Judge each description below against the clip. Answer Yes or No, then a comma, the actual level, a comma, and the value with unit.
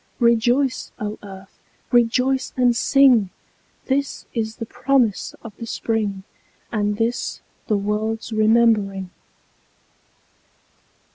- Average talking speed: No, slow, 95 wpm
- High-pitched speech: Yes, high, 225 Hz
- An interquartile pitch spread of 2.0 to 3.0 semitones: Yes, average, 2.7 semitones